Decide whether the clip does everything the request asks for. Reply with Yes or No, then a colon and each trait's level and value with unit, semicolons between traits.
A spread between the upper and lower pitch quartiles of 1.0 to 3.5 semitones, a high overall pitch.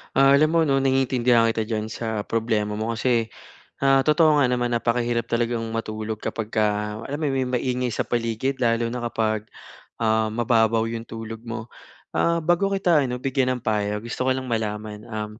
No: average, 2.8 semitones; low, 115 Hz